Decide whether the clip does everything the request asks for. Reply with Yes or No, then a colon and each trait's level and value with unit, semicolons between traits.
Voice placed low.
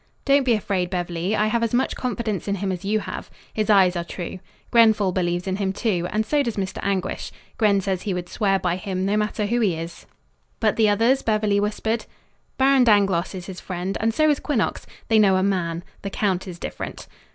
No: high, 200 Hz